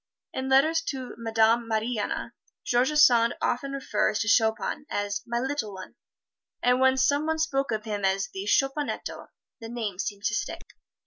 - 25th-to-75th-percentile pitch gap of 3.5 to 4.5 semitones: Yes, average, 4.0 semitones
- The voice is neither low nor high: No, high, 235 Hz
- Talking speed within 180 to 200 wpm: No, average, 165 wpm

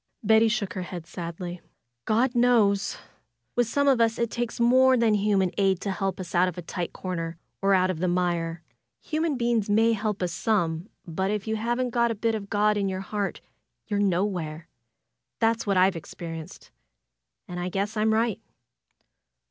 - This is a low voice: No, high, 200 Hz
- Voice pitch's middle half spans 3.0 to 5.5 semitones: Yes, average, 4.0 semitones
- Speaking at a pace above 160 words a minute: Yes, average, 185 wpm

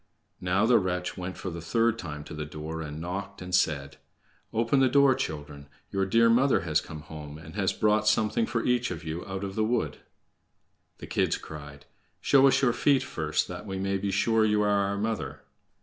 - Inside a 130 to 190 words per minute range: No, fast, 205 wpm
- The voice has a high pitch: No, very low, 95 Hz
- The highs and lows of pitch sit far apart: Yes, wide, 6.1 semitones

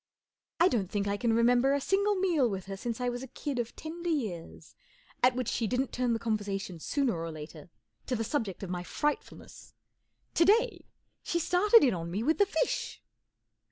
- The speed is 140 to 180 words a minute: No, average, 200 wpm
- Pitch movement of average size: No, wide, 7.1 semitones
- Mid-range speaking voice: No, high, 245 Hz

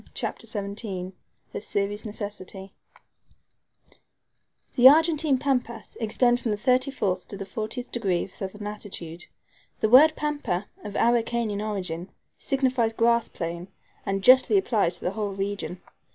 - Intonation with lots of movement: No, average, 4.0 semitones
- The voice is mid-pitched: No, high, 215 Hz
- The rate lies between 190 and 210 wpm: No, slow, 135 wpm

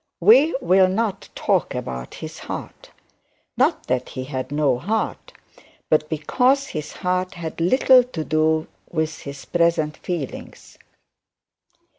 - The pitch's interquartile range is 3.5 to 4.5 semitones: Yes, average, 4.1 semitones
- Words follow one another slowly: Yes, slow, 125 wpm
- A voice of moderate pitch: Yes, medium, 160 Hz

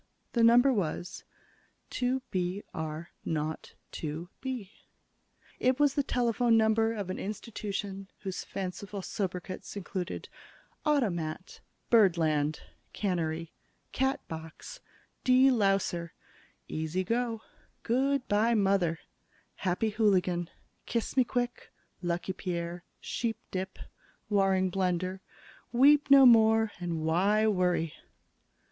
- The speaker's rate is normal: No, slow, 100 wpm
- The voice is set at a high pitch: Yes, high, 195 Hz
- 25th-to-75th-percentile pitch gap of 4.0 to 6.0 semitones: Yes, average, 4.8 semitones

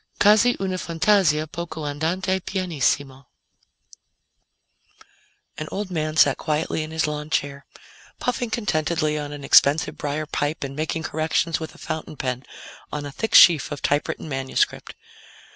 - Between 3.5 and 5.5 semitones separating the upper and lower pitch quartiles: No, average, 2.8 semitones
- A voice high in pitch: No, medium, 155 Hz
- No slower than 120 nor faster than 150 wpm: Yes, slow, 135 wpm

